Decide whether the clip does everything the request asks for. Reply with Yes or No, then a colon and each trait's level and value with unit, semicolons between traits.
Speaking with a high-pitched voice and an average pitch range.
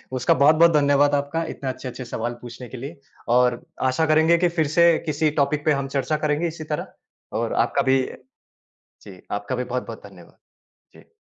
No: medium, 140 Hz; average, 3.7 semitones